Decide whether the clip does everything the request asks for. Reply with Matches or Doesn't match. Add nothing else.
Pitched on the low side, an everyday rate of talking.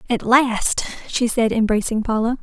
Doesn't match